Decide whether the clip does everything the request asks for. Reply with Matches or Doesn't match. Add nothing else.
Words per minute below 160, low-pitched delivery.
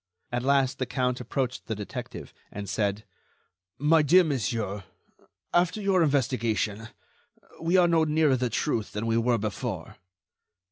Matches